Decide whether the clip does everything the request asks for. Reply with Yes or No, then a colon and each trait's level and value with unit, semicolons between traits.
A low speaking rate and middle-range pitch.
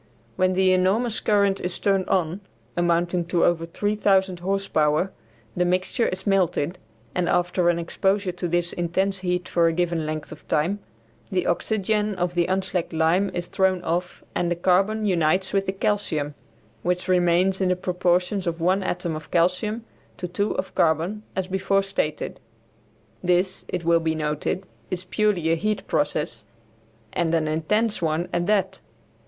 No: average, 165 wpm; medium, 180 Hz